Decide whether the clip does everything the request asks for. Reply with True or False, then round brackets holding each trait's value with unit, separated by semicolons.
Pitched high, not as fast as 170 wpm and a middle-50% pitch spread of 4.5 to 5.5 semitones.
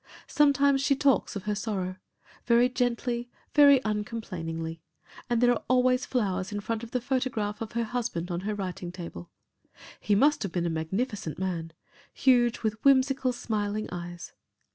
True (220 Hz; 160 wpm; 5.1 semitones)